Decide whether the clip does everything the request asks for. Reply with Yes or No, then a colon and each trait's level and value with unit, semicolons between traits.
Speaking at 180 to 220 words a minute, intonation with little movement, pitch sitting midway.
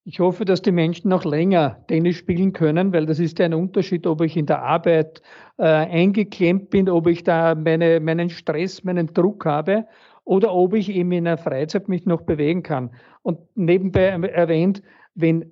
Yes: average, 185 wpm; narrow, 2.3 semitones; medium, 175 Hz